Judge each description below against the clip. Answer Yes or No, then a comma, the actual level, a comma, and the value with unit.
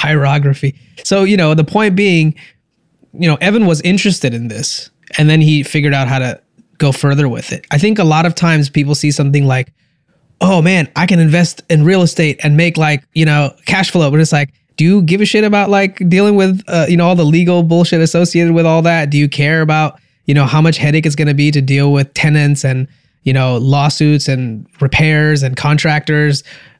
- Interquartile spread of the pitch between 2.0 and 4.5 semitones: Yes, average, 3.1 semitones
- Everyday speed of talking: No, fast, 220 wpm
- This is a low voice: No, medium, 155 Hz